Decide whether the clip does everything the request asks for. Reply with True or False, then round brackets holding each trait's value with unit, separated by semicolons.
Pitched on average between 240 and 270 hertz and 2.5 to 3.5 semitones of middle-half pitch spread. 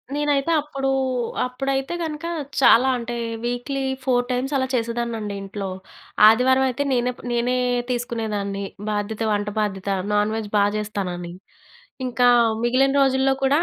False (245 Hz; 4.2 semitones)